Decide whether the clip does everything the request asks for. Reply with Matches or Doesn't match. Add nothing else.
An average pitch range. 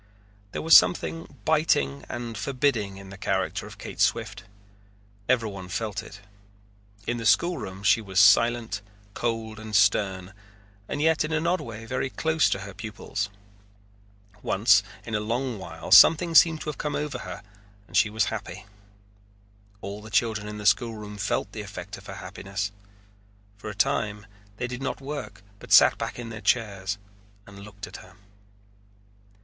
Matches